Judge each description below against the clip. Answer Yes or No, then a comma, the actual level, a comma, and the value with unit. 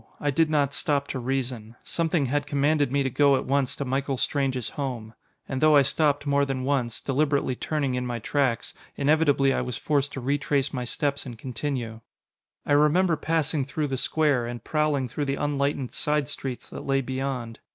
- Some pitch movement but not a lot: No, narrow, 2.2 semitones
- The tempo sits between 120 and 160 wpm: No, average, 190 wpm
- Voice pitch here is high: No, medium, 140 Hz